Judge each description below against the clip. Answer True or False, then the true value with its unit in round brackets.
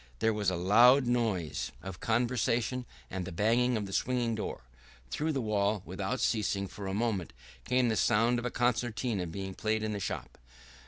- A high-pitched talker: False (110 Hz)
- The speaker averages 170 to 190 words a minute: True (180 wpm)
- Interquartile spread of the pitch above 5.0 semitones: False (3.8 semitones)